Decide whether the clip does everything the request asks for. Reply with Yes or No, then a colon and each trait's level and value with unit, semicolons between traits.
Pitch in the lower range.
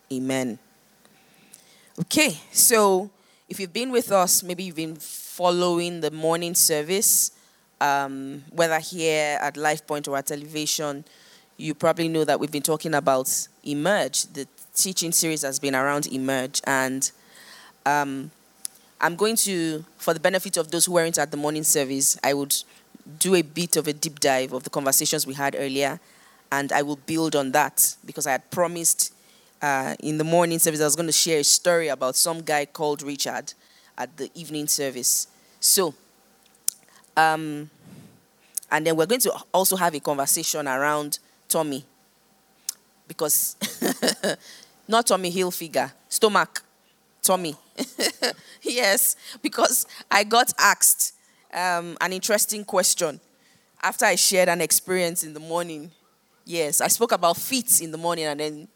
No: medium, 160 Hz